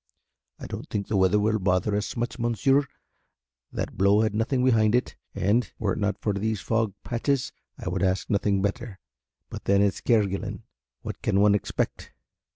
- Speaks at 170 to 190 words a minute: Yes, average, 175 wpm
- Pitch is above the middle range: No, low, 105 Hz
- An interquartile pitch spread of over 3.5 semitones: No, narrow, 2.6 semitones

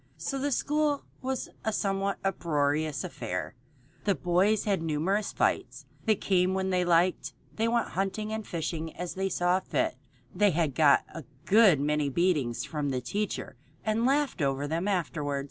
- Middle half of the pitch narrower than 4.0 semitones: No, average, 5.3 semitones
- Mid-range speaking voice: Yes, medium, 180 Hz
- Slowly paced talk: No, average, 160 wpm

